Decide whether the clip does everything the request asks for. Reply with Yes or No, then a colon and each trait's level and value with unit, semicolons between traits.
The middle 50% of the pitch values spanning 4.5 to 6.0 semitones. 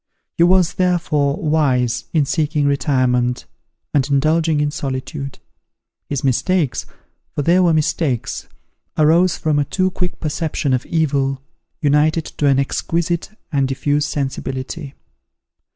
No: average, 3.2 semitones